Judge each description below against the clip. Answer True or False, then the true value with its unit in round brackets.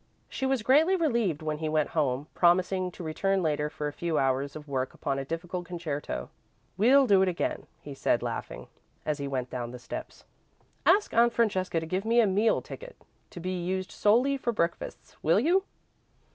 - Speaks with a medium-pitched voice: True (175 Hz)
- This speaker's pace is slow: False (190 wpm)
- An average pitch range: False (7.0 semitones)